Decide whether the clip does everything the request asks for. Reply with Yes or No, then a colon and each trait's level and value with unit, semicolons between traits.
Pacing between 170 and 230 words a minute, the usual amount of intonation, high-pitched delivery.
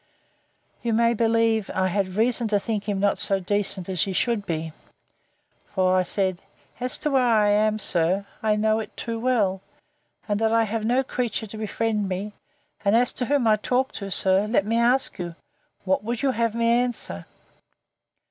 Yes: average, 185 wpm; average, 3.1 semitones; high, 215 Hz